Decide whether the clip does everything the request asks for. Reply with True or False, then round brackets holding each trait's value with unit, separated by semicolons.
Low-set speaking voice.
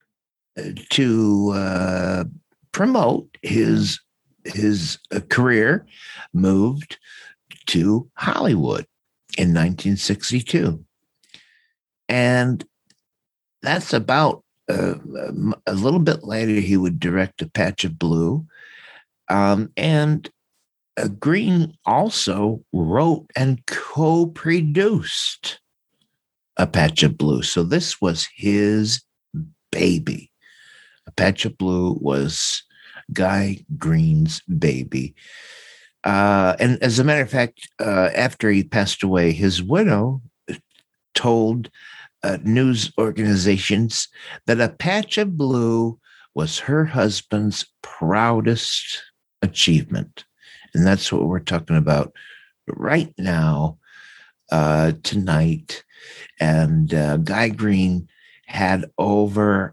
True (105 Hz)